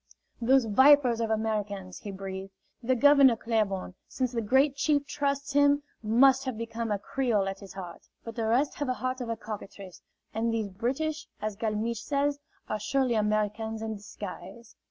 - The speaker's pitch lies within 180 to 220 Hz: No, high, 230 Hz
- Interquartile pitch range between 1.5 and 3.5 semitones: No, average, 4.2 semitones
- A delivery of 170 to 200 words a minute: Yes, average, 175 wpm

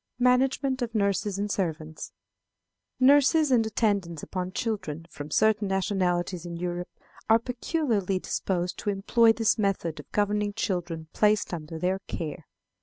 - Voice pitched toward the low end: No, high, 200 Hz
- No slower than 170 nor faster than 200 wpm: No, slow, 135 wpm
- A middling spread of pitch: Yes, average, 4.2 semitones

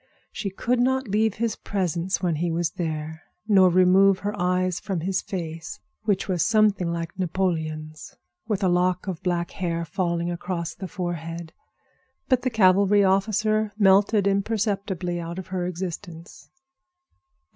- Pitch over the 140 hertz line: Yes, medium, 185 Hz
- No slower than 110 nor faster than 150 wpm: Yes, average, 145 wpm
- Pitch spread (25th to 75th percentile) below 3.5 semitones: Yes, average, 2.8 semitones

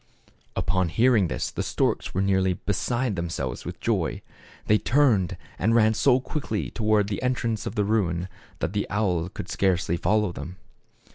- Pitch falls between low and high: No, low, 105 Hz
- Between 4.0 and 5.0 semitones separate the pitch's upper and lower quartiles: No, average, 3.5 semitones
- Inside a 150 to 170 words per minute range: Yes, average, 165 wpm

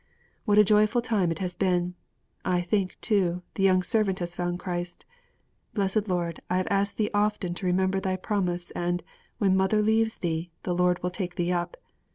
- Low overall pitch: No, medium, 185 Hz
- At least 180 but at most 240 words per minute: Yes, average, 190 wpm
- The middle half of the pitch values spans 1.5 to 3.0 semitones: Yes, narrow, 2.6 semitones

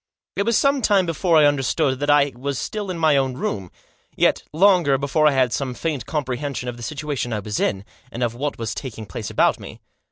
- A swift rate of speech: Yes, fast, 220 wpm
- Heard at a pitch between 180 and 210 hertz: No, medium, 140 Hz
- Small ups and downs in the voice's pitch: No, average, 4.3 semitones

